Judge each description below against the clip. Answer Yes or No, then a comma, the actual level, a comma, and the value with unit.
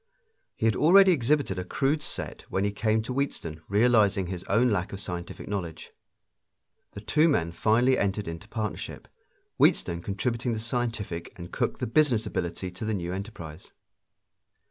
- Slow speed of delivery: No, average, 160 wpm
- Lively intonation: No, average, 4.9 semitones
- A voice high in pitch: No, low, 105 Hz